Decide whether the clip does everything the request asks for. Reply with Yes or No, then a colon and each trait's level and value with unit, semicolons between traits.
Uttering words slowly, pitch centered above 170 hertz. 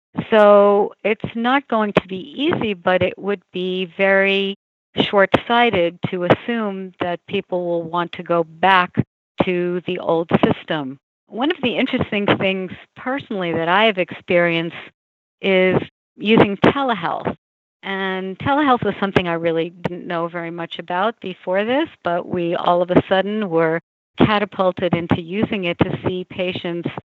No: average, 150 wpm; medium, 185 Hz